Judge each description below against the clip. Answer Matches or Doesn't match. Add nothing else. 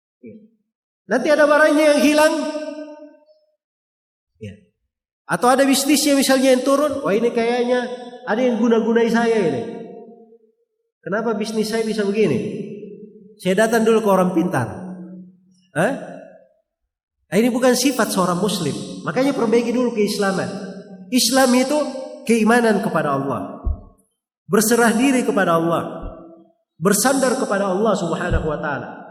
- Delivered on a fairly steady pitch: Doesn't match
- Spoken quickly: Doesn't match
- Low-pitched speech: Doesn't match